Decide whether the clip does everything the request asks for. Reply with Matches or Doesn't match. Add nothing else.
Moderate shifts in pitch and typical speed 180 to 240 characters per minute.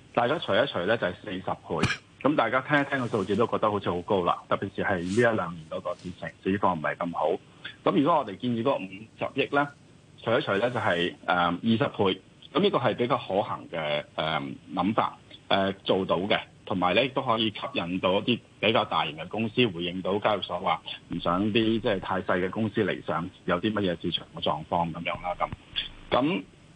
Doesn't match